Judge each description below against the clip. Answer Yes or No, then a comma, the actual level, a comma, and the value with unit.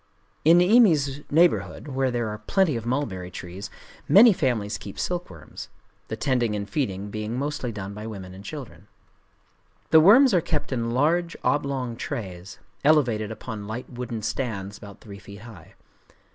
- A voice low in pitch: Yes, low, 120 Hz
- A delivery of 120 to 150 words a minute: Yes, average, 145 wpm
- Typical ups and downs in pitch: No, wide, 6.3 semitones